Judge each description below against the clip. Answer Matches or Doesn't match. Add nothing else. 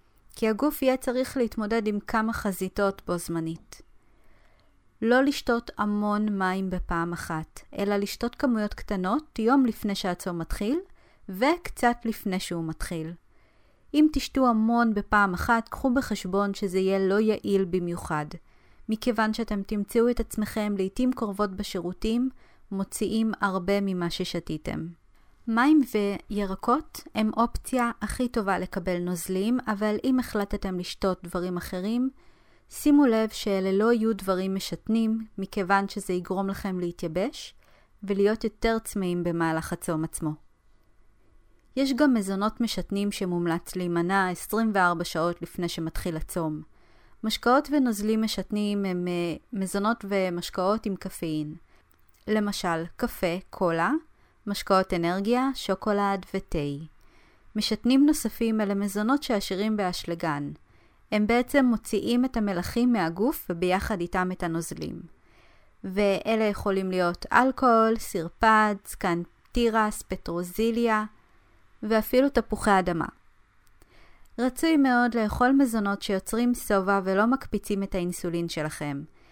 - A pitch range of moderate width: Matches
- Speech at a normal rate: Matches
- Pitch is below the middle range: Doesn't match